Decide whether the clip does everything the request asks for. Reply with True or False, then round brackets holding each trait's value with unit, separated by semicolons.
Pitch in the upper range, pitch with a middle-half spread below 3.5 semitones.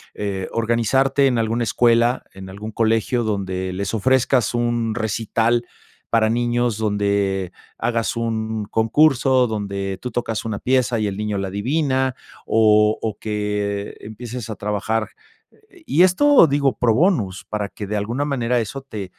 False (110 Hz; 2.9 semitones)